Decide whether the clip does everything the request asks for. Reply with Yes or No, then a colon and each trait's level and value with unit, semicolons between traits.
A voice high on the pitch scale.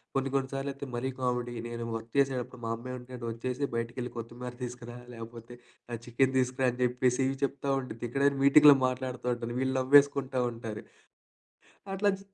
No: low, 125 Hz